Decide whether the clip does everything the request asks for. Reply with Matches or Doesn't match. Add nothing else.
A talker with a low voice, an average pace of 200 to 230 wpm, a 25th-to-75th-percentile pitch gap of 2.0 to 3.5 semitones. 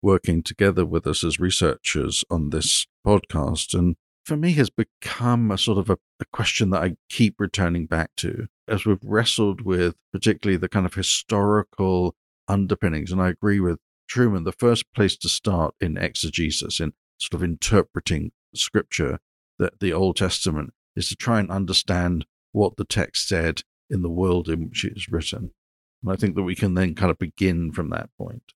Doesn't match